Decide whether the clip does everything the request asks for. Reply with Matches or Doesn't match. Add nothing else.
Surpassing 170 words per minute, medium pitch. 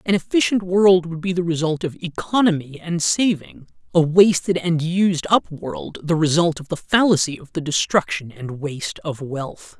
Matches